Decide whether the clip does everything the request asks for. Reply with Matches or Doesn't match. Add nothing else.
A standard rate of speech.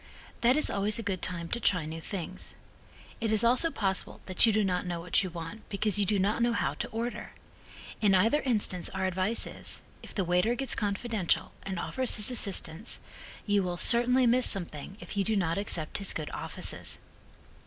Matches